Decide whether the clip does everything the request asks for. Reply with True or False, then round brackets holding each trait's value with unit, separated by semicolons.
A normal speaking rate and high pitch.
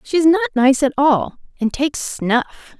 True (195 wpm; 285 Hz)